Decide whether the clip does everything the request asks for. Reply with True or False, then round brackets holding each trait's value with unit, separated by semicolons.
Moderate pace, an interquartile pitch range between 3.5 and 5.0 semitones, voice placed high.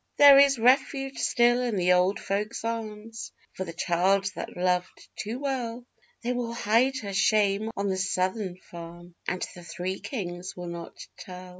True (165 wpm; 4.4 semitones; 200 Hz)